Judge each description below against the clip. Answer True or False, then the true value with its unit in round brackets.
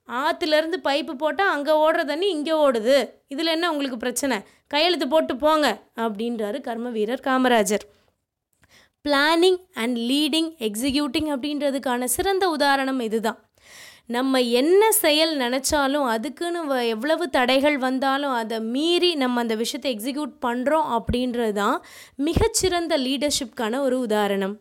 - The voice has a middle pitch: False (280 Hz)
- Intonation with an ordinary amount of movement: True (4.5 semitones)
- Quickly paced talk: False (115 wpm)